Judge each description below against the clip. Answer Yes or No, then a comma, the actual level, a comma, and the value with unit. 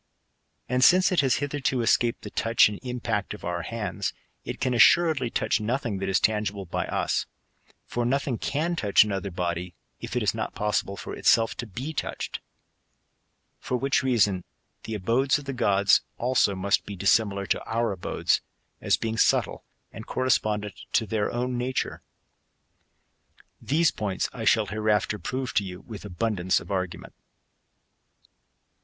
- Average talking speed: Yes, average, 155 wpm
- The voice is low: Yes, low, 110 Hz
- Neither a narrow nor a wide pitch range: Yes, average, 4.3 semitones